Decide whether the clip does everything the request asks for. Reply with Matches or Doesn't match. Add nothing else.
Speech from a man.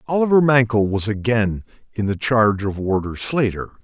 Matches